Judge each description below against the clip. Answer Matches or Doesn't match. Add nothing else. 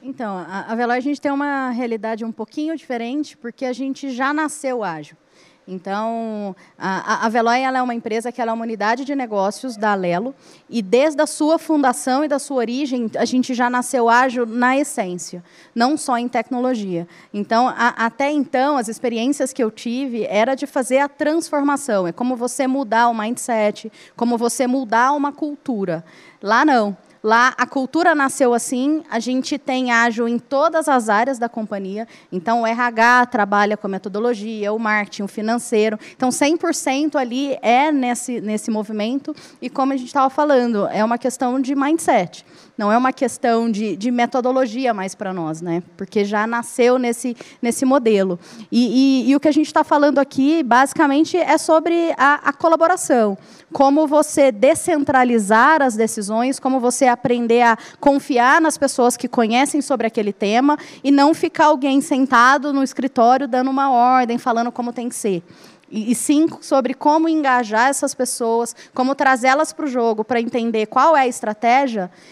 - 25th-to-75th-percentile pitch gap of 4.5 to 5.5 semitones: Doesn't match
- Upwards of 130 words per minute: Matches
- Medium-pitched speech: Doesn't match